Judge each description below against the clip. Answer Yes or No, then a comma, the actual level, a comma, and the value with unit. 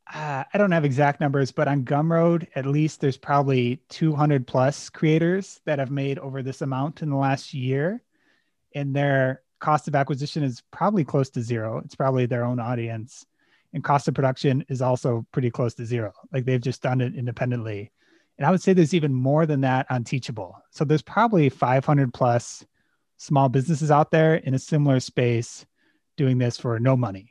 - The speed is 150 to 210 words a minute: Yes, average, 190 wpm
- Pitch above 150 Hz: No, medium, 140 Hz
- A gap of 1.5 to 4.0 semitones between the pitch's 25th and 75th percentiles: Yes, average, 3.1 semitones